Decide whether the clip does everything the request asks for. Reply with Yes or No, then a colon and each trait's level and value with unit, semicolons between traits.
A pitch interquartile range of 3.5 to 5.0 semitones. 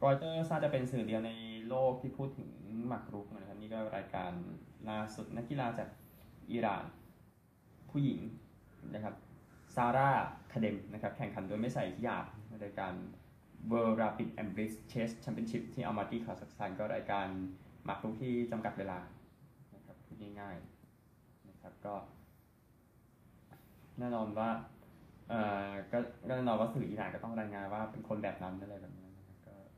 No: average, 2.9 semitones